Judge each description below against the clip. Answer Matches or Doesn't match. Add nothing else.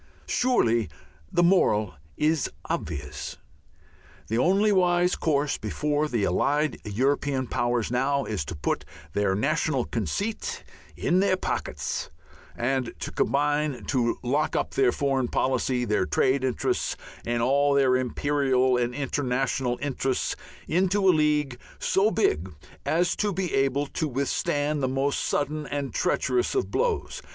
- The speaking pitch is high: Doesn't match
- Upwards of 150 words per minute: Doesn't match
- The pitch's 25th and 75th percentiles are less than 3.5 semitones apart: Doesn't match